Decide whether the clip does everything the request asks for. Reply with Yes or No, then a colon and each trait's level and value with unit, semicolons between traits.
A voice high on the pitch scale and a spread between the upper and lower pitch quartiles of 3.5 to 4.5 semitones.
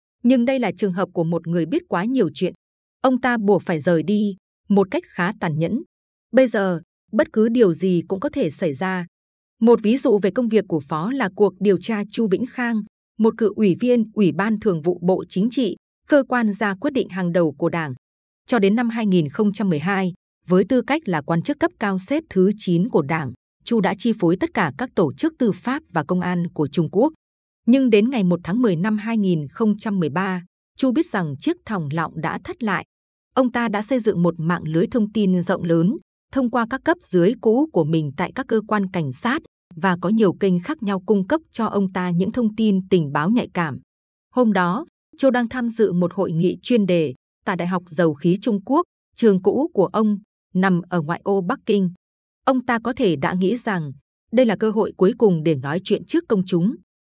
No: high, 200 Hz; average, 4.9 semitones